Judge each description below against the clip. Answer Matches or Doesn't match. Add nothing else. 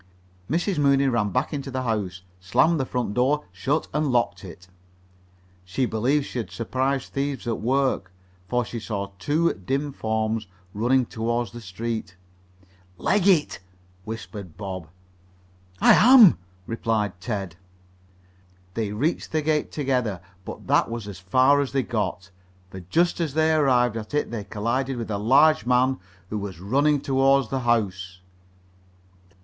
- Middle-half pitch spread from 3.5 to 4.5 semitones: Doesn't match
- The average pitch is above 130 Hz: Doesn't match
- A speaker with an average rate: Matches